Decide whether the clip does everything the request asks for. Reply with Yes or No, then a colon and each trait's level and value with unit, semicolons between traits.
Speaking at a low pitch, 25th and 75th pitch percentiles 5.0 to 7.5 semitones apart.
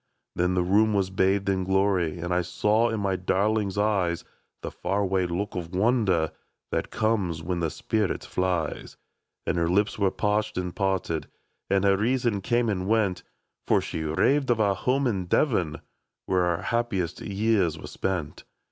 No: very low, 95 Hz; average, 3.1 semitones